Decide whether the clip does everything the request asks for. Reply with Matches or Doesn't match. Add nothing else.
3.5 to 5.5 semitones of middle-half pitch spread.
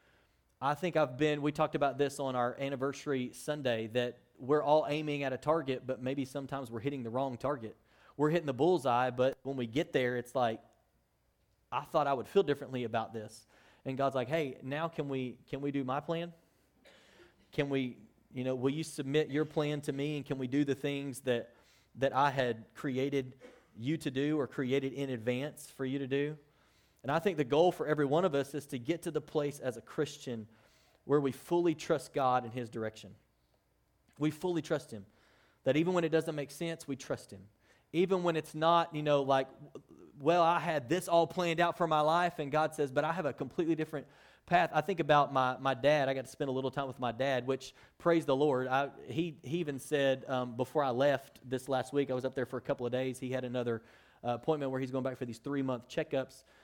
Doesn't match